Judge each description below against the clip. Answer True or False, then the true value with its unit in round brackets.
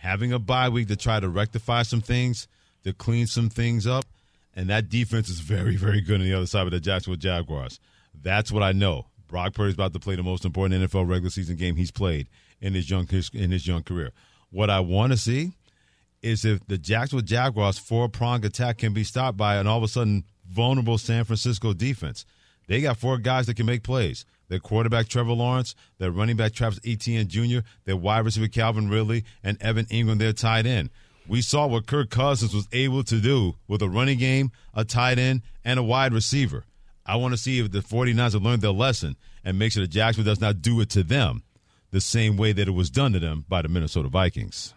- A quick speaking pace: True (220 wpm)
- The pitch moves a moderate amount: True (3.8 semitones)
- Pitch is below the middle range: True (110 Hz)